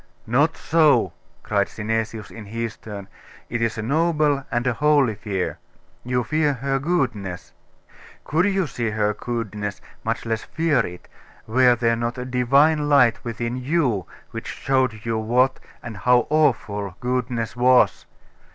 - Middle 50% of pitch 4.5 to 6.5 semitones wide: No, average, 3.8 semitones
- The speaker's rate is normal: Yes, average, 145 wpm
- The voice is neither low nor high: No, low, 120 Hz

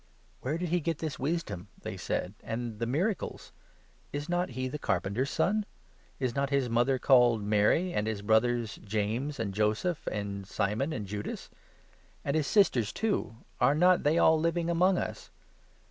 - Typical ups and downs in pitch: No, wide, 7.0 semitones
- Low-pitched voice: Yes, low, 130 Hz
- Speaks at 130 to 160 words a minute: No, average, 175 wpm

